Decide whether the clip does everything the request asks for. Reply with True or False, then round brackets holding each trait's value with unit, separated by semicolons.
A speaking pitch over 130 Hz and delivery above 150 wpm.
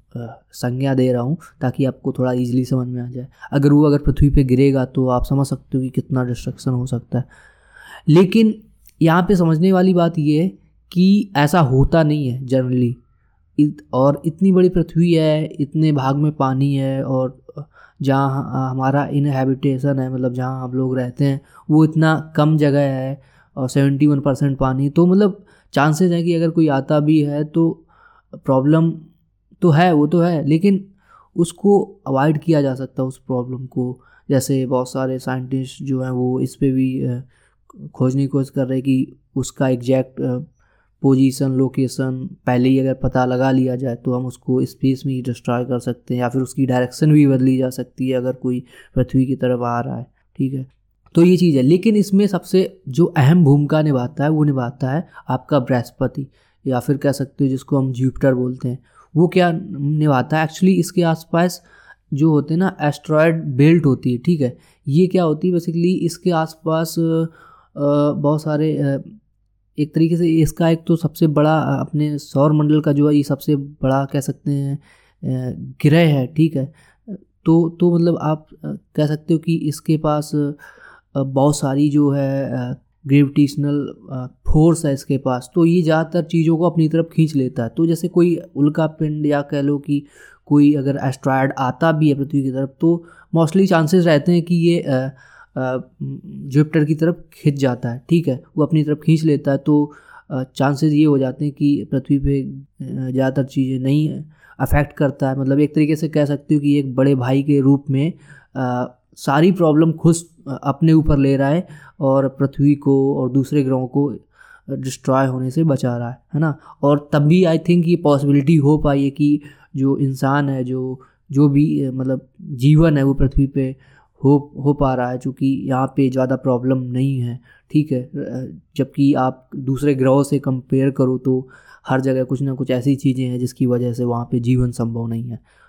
True (140 Hz; 185 wpm)